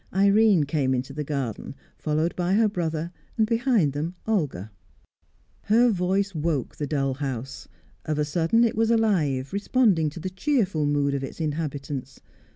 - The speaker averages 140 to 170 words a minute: Yes, average, 160 wpm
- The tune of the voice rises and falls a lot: Yes, wide, 5.9 semitones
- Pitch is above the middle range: No, medium, 160 Hz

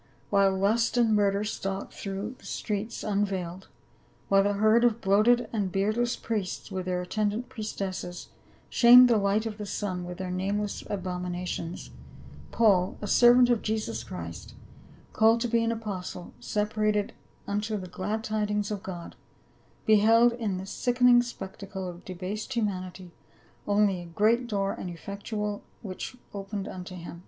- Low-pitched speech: No, high, 205 Hz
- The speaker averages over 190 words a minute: No, average, 150 wpm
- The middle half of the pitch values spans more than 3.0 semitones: No, average, 2.7 semitones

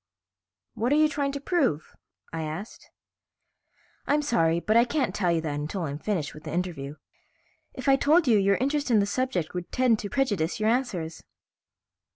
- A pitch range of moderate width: No, wide, 8.7 semitones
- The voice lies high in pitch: Yes, high, 210 Hz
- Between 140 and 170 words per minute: No, average, 185 wpm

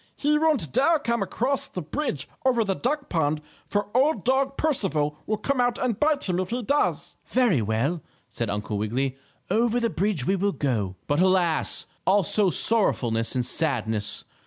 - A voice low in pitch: No, high, 195 Hz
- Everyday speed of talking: Yes, average, 170 wpm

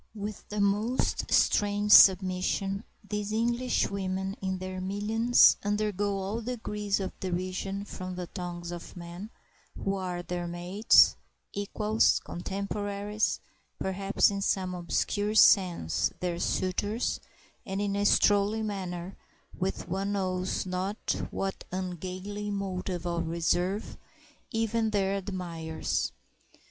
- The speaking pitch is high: Yes, high, 195 Hz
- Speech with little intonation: Yes, narrow, 2.1 semitones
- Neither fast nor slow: No, slow, 110 wpm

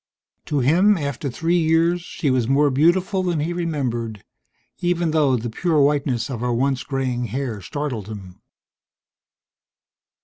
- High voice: No, medium, 140 Hz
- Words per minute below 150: Yes, average, 140 wpm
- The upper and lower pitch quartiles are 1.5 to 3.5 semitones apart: No, average, 5.2 semitones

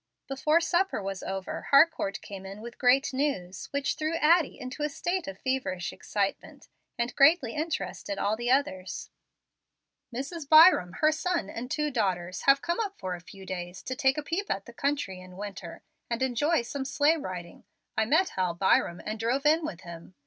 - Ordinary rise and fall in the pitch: No, wide, 7.7 semitones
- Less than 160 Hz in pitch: No, very high, 250 Hz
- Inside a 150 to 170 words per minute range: No, average, 185 wpm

